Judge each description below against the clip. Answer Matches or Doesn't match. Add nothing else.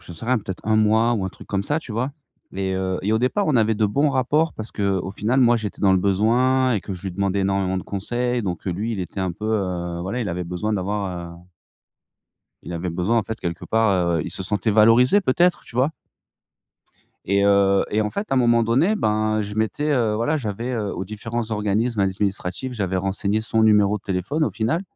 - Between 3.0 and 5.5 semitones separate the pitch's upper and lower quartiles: Matches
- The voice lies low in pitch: Matches